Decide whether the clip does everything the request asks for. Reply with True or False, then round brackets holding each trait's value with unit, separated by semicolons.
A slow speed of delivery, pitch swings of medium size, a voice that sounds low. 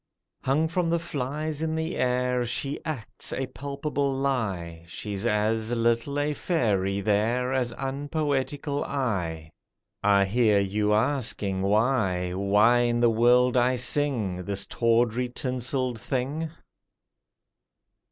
True (115 wpm; 4.8 semitones; 125 Hz)